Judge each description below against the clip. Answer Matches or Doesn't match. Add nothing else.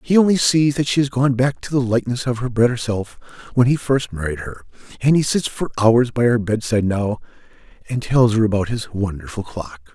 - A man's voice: Matches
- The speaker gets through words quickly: Matches